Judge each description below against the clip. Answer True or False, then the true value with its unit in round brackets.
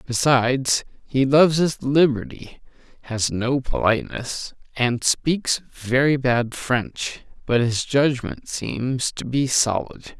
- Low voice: True (130 Hz)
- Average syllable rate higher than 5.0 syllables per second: False (3.5 syllables/s)